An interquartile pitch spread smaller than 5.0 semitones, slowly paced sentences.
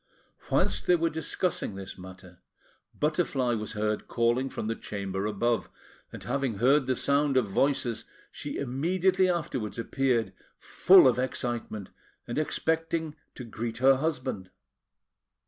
No: wide, 5.6 semitones; slow, 130 wpm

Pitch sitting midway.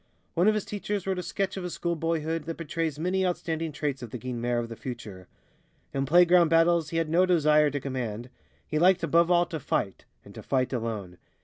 Yes: medium, 160 Hz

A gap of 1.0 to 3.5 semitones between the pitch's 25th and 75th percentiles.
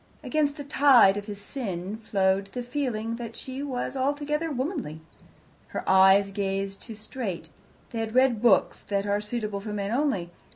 No: average, 5.0 semitones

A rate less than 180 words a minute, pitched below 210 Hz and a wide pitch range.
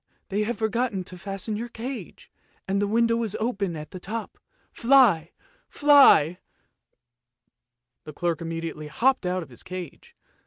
Yes: average, 150 wpm; high, 190 Hz; wide, 5.9 semitones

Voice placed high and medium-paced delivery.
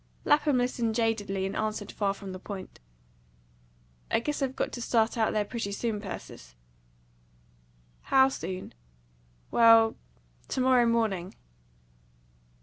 No: high, 225 Hz; slow, 125 wpm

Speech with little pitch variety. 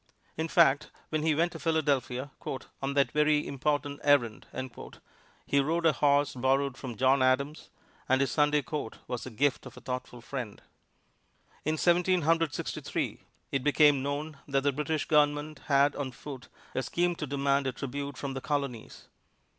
Yes: narrow, 2.2 semitones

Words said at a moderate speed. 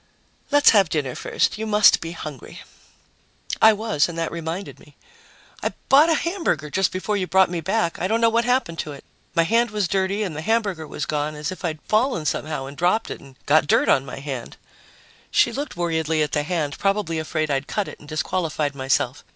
No: fast, 210 wpm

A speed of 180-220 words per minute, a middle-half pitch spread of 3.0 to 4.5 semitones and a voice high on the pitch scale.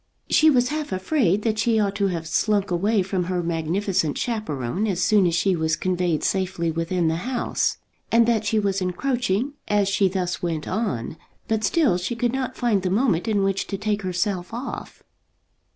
Yes: average, 185 wpm; average, 3.9 semitones; high, 195 Hz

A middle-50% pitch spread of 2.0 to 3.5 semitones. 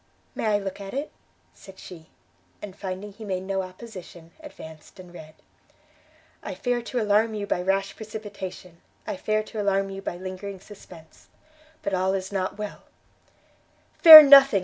Yes: narrow, 2.5 semitones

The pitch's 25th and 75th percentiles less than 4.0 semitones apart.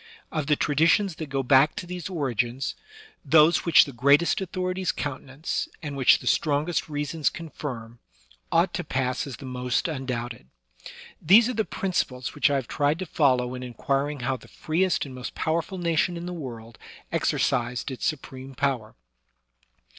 No: average, 4.4 semitones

